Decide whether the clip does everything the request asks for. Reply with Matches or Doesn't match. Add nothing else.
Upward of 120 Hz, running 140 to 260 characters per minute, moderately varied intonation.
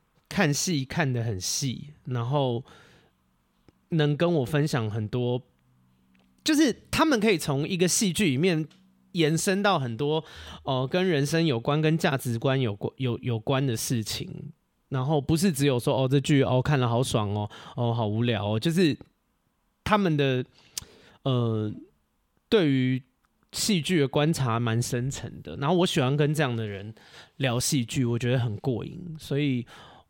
Matches